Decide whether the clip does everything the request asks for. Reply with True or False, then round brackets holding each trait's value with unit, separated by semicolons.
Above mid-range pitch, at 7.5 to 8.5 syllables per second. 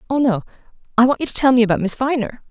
True (245 Hz; 7.6 syllables/s)